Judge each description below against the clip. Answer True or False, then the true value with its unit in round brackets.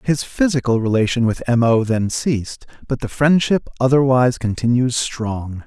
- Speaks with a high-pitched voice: False (125 Hz)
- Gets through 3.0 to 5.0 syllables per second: True (4.8 syllables/s)